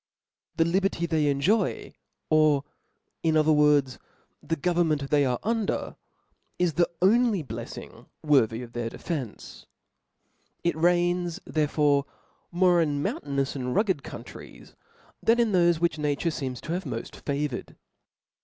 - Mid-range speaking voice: Yes, medium, 155 Hz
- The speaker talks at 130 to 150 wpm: Yes, slow, 135 wpm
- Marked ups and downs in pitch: No, average, 3.8 semitones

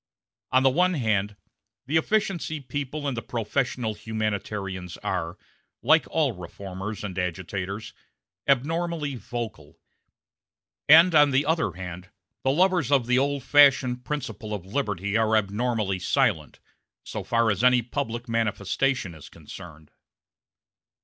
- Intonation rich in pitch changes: Yes, wide, 6.1 semitones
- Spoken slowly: Yes, slow, 125 wpm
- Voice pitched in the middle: No, low, 120 Hz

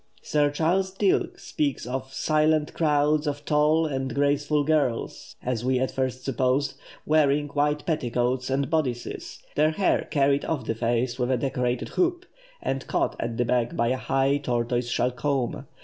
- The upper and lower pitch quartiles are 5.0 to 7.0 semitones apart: No, average, 3.1 semitones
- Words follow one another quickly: No, average, 165 wpm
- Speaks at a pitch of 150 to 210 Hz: No, medium, 140 Hz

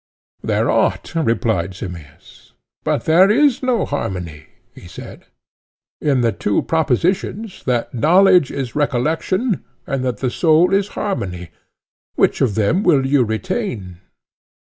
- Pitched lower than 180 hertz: Yes, medium, 140 Hz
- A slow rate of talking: Yes, slow, 130 wpm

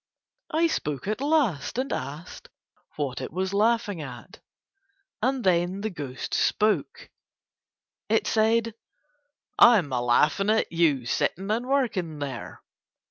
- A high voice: Yes, high, 195 Hz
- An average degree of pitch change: No, wide, 7.6 semitones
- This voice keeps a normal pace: No, slow, 125 wpm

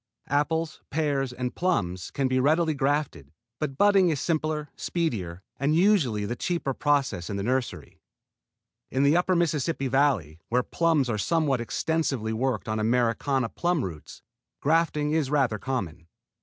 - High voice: No, low, 135 Hz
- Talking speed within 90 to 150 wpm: Yes, average, 145 wpm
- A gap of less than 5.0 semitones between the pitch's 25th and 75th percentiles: No, average, 5.3 semitones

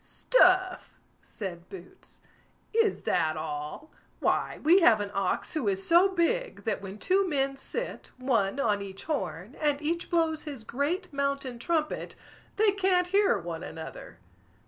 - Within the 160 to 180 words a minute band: No, average, 145 wpm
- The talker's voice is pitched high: Yes, very high, 280 Hz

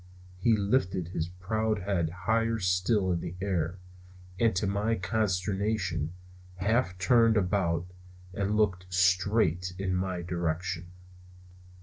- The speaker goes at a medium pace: No, slow, 115 wpm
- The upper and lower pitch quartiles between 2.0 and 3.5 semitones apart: Yes, average, 3.0 semitones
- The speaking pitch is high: No, very low, 95 Hz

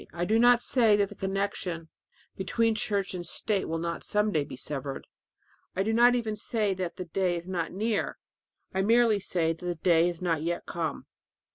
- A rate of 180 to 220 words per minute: Yes, average, 200 wpm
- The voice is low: No, high, 190 Hz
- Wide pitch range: No, average, 4.0 semitones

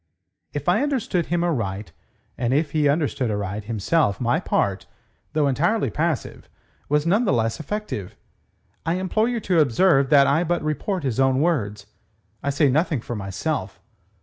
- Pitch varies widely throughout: Yes, wide, 6.8 semitones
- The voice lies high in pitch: No, medium, 145 Hz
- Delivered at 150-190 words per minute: Yes, average, 155 wpm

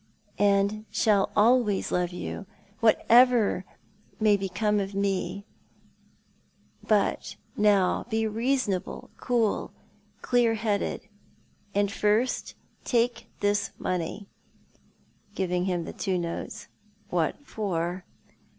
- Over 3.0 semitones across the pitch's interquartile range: No, average, 2.7 semitones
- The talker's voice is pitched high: Yes, high, 205 Hz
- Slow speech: Yes, slow, 95 wpm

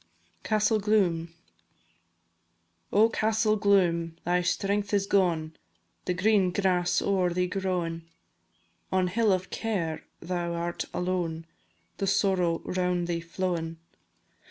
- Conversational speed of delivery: No, slow, 110 wpm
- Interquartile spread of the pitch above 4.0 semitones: No, average, 2.8 semitones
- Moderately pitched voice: Yes, medium, 180 Hz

